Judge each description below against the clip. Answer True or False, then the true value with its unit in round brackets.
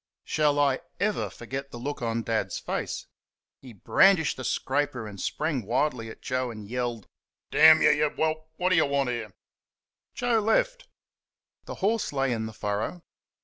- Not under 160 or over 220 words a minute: True (165 wpm)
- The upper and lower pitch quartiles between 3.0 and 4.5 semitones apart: False (5.2 semitones)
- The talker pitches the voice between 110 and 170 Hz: True (135 Hz)